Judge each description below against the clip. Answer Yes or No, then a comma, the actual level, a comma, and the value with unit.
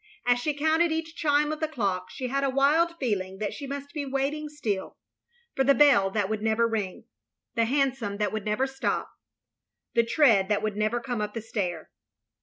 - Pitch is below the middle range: No, high, 245 Hz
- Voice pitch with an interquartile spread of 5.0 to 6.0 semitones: Yes, wide, 5.5 semitones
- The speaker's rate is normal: No, fast, 210 wpm